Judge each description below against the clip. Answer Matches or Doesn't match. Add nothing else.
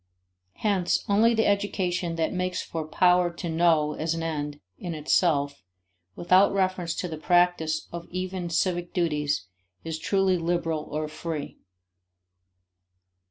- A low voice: Doesn't match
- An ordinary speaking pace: Doesn't match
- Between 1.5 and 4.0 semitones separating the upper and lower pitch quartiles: Matches